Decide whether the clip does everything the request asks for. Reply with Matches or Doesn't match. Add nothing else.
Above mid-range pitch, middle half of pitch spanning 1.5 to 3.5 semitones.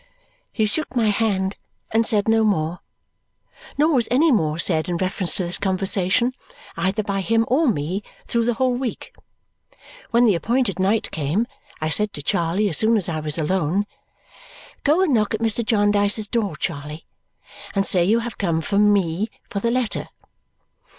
Doesn't match